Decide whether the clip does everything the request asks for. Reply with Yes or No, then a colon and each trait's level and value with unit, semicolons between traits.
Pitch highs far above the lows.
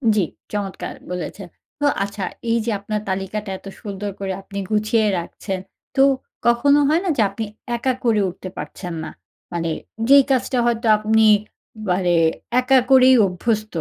No: average, 3.6 semitones